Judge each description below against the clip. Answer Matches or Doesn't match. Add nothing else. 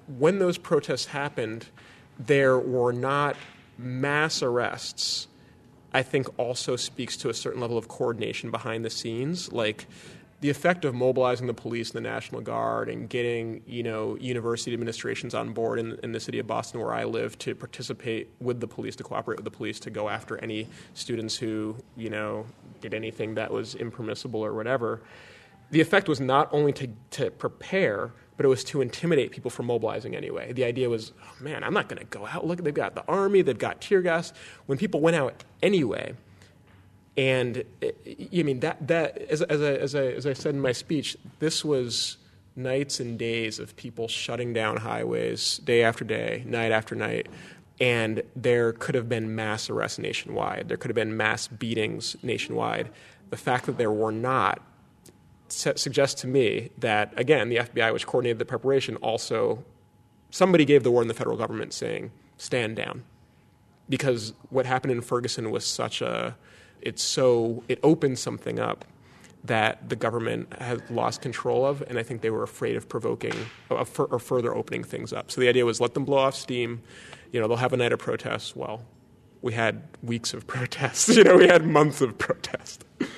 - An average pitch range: Matches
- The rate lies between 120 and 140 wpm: Doesn't match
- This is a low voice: Matches